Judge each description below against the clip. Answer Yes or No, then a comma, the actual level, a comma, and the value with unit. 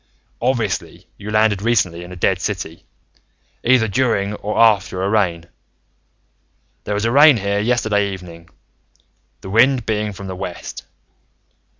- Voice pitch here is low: Yes, low, 105 Hz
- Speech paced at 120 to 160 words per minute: Yes, slow, 135 wpm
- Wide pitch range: No, average, 3.1 semitones